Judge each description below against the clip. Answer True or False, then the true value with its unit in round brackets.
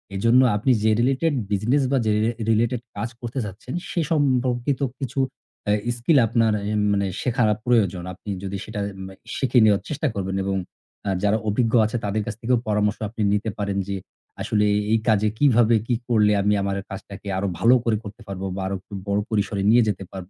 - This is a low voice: True (110 Hz)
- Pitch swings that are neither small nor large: True (3.3 semitones)